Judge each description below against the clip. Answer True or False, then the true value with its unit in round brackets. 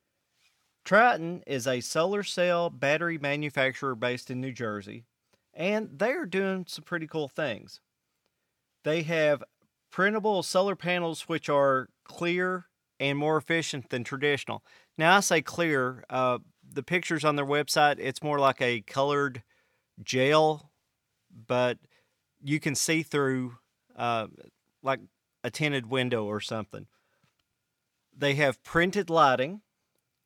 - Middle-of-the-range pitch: True (145 Hz)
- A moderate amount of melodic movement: True (4.6 semitones)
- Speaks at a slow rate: True (125 wpm)